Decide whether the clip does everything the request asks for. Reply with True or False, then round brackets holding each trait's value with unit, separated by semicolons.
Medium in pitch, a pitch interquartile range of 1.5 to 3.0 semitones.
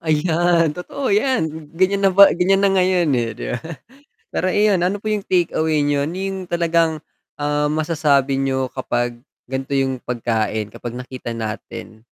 False (155 Hz; 5.6 semitones)